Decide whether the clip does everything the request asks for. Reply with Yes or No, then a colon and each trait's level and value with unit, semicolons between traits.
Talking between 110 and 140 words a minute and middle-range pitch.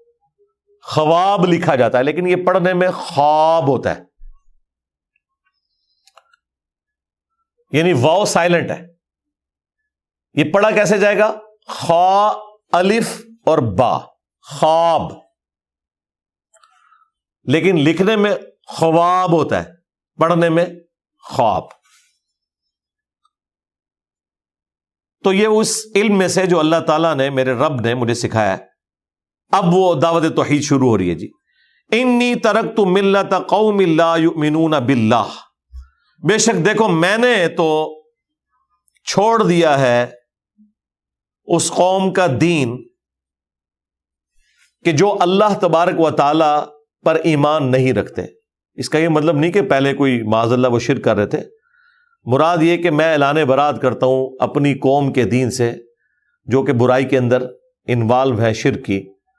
Yes: average, 125 wpm; medium, 165 Hz